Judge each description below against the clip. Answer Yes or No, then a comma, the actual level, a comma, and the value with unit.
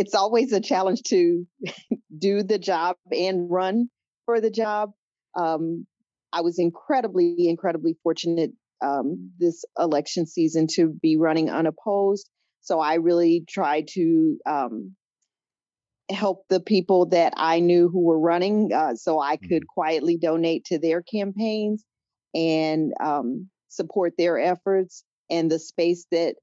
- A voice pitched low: No, medium, 175 Hz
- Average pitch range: Yes, average, 3.3 semitones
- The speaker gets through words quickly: No, slow, 135 wpm